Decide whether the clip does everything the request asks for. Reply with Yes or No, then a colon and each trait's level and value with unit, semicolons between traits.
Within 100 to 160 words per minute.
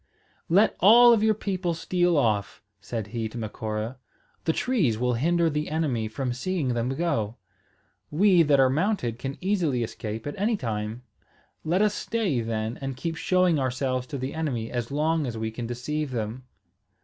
No: average, 175 wpm